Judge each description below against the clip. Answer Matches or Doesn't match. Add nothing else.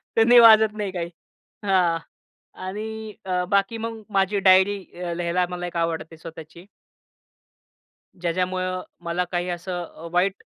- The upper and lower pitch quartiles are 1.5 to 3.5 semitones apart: Matches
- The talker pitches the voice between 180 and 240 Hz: Matches